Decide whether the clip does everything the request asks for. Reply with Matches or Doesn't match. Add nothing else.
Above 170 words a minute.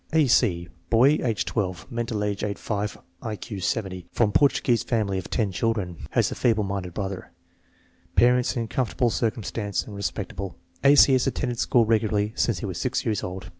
Matches